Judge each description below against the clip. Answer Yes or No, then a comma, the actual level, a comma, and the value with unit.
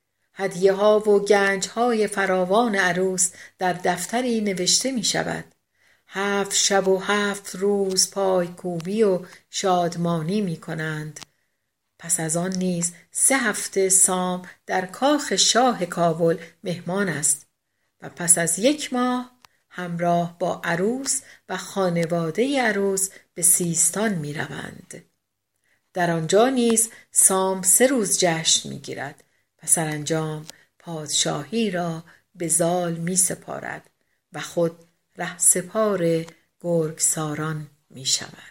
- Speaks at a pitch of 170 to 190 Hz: Yes, medium, 185 Hz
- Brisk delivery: No, average, 120 wpm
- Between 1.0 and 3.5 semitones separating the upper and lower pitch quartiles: Yes, average, 3.0 semitones